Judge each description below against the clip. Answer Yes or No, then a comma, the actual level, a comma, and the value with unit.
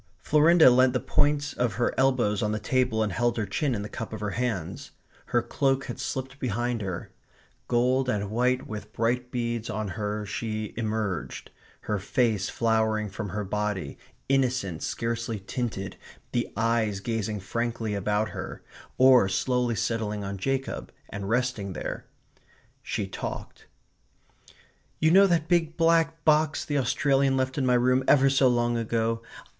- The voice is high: No, low, 115 Hz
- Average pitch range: Yes, average, 3.6 semitones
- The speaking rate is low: No, average, 155 wpm